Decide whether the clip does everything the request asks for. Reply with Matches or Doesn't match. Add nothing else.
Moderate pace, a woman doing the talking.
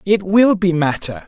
Doesn't match